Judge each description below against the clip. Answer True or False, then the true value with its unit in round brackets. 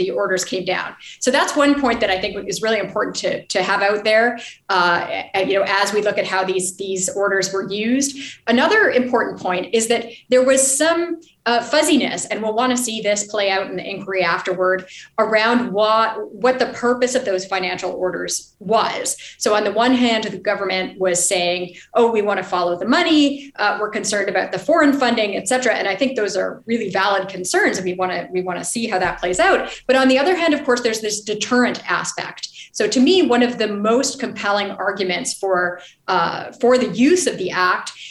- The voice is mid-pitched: False (215 Hz)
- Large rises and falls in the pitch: False (4.4 semitones)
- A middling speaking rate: False (215 wpm)